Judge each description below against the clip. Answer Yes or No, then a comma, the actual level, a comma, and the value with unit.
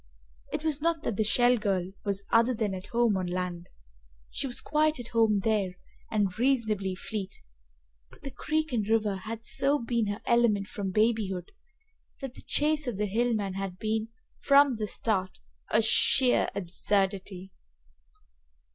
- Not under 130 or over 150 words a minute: No, average, 160 wpm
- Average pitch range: Yes, average, 3.8 semitones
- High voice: Yes, high, 215 Hz